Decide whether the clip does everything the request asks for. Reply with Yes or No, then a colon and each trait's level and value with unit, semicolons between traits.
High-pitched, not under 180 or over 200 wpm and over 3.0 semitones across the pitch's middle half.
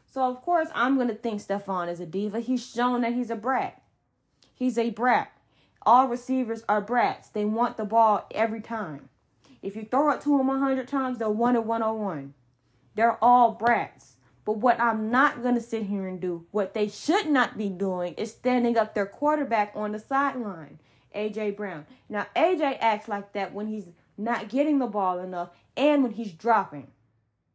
Yes: high, 225 Hz; average, 190 wpm; average, 3.6 semitones